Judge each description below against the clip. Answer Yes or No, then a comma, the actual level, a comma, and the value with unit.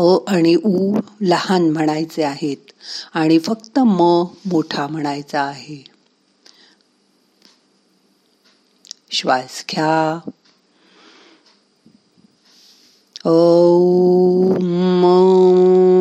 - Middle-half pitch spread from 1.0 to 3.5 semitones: Yes, average, 2.8 semitones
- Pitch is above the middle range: No, medium, 175 Hz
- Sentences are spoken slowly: Yes, slow, 55 wpm